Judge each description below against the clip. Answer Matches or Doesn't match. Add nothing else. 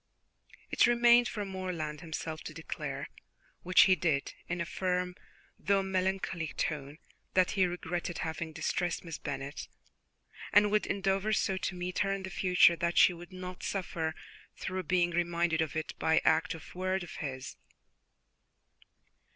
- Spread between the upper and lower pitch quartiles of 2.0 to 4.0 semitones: Matches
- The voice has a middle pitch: Matches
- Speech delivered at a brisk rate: Doesn't match